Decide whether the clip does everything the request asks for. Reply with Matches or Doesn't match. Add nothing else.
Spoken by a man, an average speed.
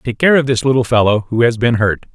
Doesn't match